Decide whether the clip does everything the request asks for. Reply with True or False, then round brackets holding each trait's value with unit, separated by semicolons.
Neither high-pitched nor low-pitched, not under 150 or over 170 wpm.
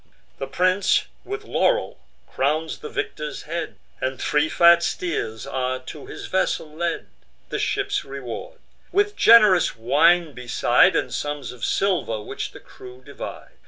False (155 Hz; 140 wpm)